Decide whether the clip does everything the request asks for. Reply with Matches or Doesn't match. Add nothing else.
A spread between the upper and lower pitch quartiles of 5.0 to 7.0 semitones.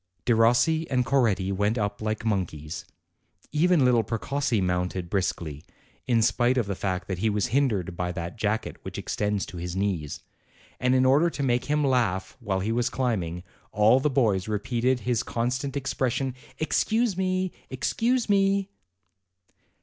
Matches